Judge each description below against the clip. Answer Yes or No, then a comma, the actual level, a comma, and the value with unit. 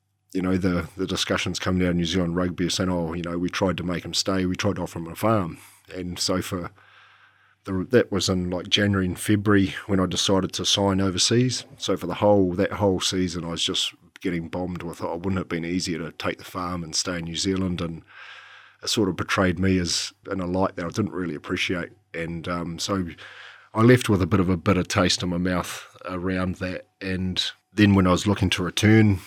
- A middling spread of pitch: No, narrow, 1.9 semitones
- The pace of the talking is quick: Yes, fast, 235 wpm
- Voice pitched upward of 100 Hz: No, very low, 90 Hz